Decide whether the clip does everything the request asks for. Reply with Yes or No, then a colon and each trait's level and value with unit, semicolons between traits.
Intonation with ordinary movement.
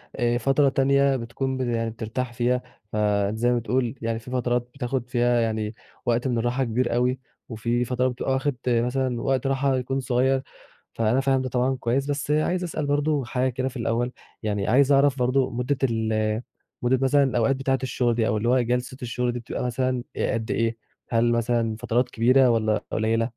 No: narrow, 2.2 semitones